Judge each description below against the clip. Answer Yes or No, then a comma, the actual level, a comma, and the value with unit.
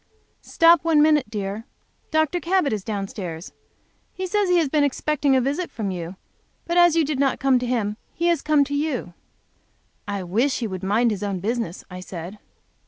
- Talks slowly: No, average, 195 wpm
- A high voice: Yes, very high, 255 Hz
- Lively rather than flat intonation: Yes, wide, 7.4 semitones